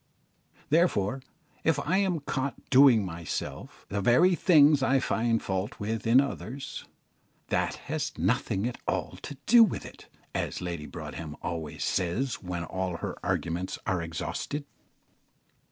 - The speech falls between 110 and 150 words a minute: Yes, slow, 135 wpm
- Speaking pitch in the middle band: No, low, 115 Hz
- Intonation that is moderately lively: No, wide, 7.7 semitones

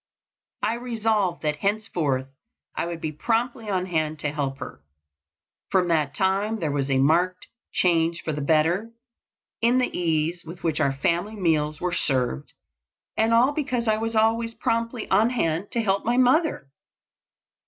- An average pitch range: No, wide, 6.4 semitones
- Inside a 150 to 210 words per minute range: Yes, average, 160 wpm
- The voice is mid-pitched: Yes, medium, 180 Hz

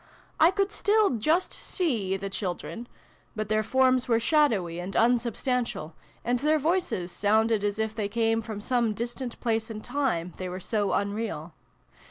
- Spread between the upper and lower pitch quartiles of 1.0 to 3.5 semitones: No, average, 4.1 semitones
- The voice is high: Yes, high, 225 Hz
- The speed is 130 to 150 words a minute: No, average, 160 wpm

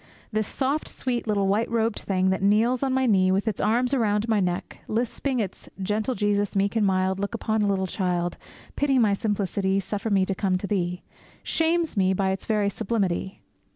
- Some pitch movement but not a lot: Yes, average, 3.2 semitones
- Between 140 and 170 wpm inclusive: No, average, 195 wpm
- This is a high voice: Yes, high, 205 Hz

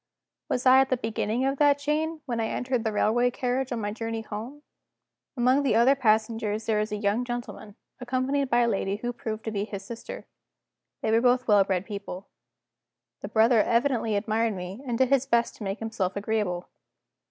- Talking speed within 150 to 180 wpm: No, average, 195 wpm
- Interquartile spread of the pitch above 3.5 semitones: No, average, 3.1 semitones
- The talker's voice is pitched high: Yes, high, 230 Hz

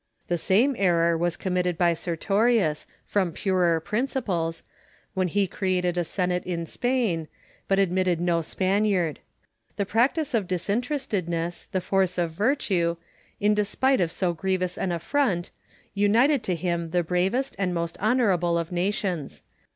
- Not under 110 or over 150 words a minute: Yes, average, 140 wpm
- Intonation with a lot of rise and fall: No, average, 3.2 semitones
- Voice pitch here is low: No, medium, 185 Hz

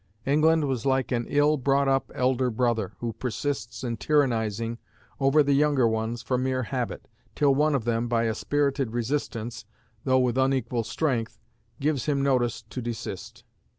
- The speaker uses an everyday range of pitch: Yes, average, 3.1 semitones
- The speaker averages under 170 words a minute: Yes, average, 160 wpm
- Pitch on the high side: No, low, 130 Hz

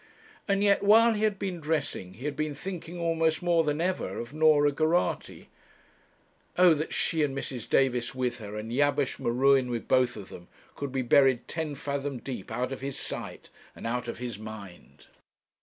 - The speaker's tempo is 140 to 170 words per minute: No, average, 185 wpm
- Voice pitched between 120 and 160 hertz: Yes, medium, 140 Hz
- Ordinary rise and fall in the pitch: Yes, average, 4.7 semitones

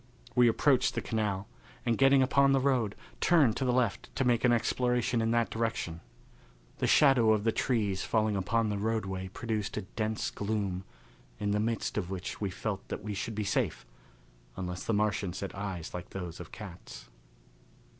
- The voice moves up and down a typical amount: Yes, average, 3.3 semitones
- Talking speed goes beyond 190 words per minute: No, average, 180 wpm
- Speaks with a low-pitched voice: Yes, low, 110 Hz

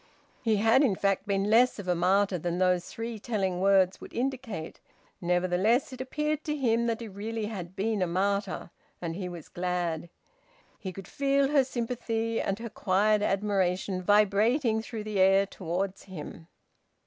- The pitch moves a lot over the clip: No, average, 3.7 semitones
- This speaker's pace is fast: No, average, 165 wpm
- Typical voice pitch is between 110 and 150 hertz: No, high, 200 Hz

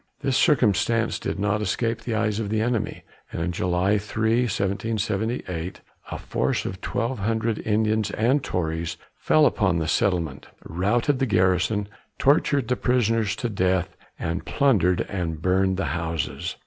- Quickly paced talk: No, average, 150 wpm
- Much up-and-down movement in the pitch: No, average, 3.9 semitones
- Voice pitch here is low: Yes, low, 105 Hz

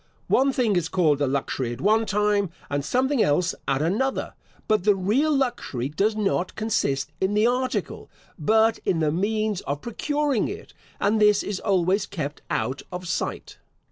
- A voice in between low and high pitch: No, high, 200 Hz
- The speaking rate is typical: Yes, average, 170 wpm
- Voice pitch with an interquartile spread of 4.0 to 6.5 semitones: Yes, wide, 5.5 semitones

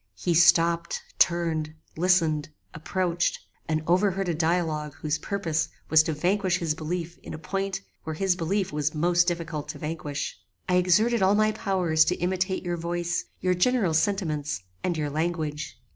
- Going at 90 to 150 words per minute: No, average, 160 wpm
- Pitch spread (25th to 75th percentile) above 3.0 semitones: No, average, 2.7 semitones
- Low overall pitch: No, medium, 170 Hz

